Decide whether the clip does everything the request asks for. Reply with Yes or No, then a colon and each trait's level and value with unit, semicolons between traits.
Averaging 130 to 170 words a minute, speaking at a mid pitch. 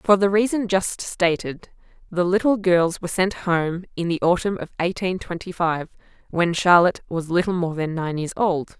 No: average, 185 wpm; medium, 180 Hz